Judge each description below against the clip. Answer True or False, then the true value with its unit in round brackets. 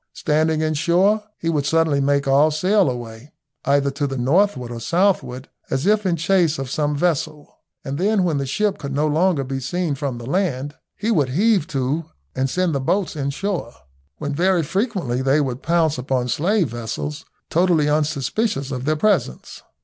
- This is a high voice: False (150 Hz)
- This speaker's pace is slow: False (180 wpm)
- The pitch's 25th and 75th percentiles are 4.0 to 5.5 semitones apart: True (4.8 semitones)